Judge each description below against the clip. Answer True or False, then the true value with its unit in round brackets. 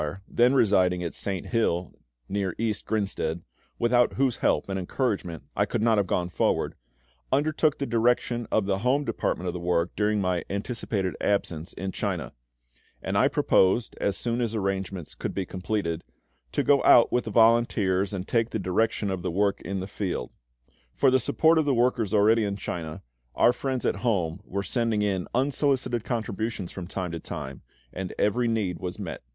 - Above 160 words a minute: True (180 wpm)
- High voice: False (100 Hz)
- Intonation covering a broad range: False (4.2 semitones)